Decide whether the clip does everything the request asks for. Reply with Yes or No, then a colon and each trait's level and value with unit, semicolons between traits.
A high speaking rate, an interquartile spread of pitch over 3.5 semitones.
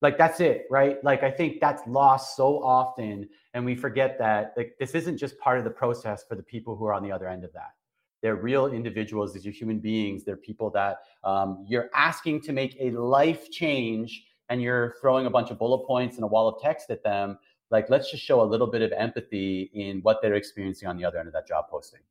Yes: fast, 240 wpm; average, 4.4 semitones